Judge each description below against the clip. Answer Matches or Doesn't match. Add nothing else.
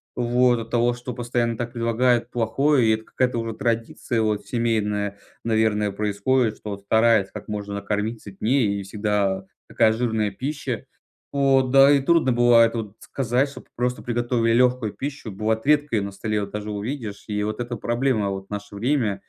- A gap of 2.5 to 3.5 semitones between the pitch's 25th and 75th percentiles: Matches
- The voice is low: Matches